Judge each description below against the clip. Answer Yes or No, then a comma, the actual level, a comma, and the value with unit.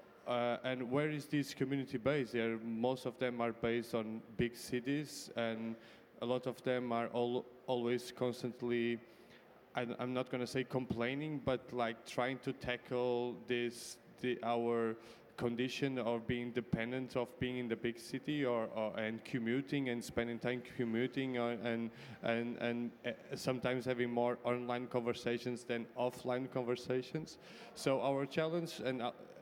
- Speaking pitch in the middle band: No, low, 125 Hz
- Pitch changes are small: Yes, narrow, 1.5 semitones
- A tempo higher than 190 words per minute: No, average, 155 wpm